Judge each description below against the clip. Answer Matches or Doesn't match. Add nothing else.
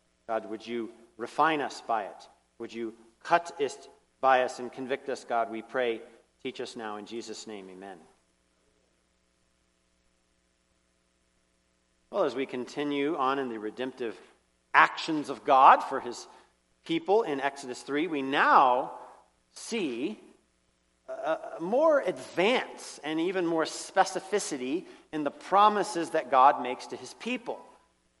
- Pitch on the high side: Doesn't match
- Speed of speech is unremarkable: Doesn't match